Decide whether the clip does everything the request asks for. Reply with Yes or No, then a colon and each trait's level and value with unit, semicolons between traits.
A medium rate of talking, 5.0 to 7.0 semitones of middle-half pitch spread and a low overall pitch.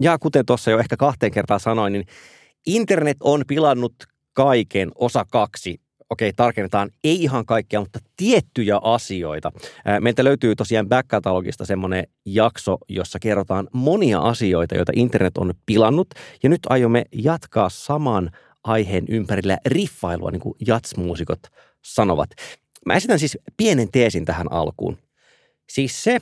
Yes: average, 135 wpm; wide, 5.5 semitones; low, 115 Hz